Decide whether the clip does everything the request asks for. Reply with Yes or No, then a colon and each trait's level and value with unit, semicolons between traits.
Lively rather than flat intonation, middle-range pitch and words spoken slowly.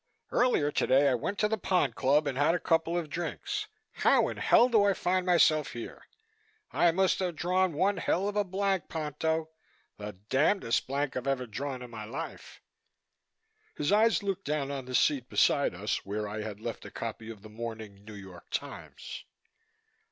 No: wide, 7.8 semitones; medium, 145 Hz; average, 185 wpm